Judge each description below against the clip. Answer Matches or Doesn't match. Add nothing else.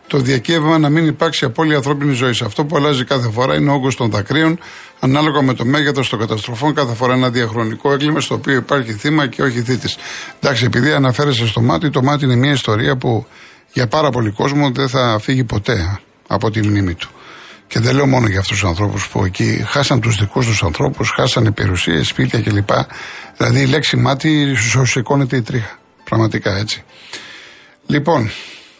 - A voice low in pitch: Matches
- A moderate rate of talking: Doesn't match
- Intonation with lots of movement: Doesn't match